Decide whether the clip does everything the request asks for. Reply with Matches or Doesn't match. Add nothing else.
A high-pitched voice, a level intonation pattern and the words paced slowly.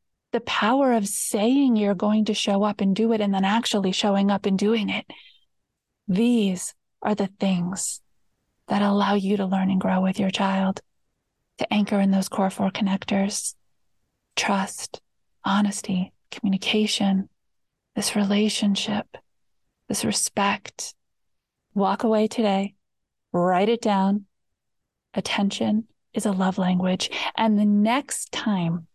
Matches